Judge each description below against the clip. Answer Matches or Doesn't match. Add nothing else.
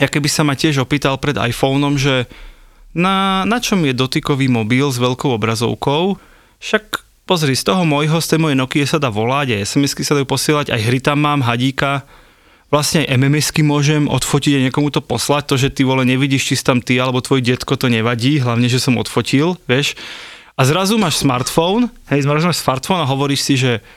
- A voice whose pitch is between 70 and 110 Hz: Doesn't match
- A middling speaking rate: Doesn't match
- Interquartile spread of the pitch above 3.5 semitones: Doesn't match